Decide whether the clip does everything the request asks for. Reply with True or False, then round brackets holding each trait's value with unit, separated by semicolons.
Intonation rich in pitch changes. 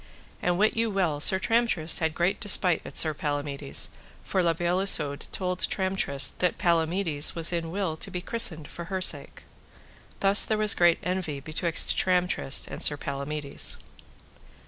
False (3.7 semitones)